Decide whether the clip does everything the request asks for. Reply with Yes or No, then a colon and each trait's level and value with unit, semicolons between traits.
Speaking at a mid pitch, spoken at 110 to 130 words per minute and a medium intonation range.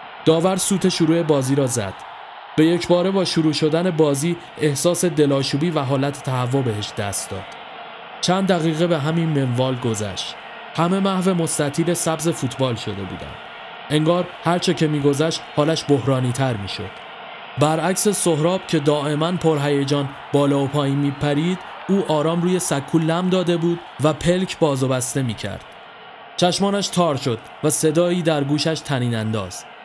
No: medium, 155 Hz; fast, 155 wpm; average, 3.8 semitones